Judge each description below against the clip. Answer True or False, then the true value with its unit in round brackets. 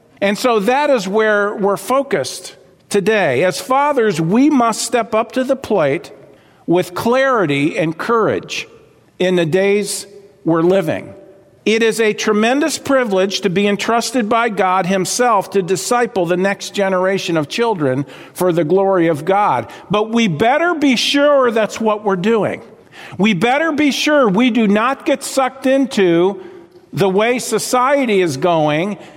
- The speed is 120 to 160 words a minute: True (150 wpm)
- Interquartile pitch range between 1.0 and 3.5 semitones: False (4.7 semitones)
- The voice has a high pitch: True (215 Hz)